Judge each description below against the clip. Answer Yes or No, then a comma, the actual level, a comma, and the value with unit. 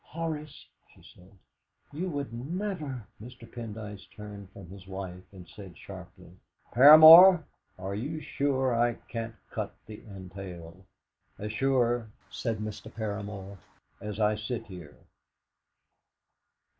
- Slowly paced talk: Yes, slow, 120 wpm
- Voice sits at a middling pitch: No, low, 110 Hz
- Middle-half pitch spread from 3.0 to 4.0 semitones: No, average, 5.3 semitones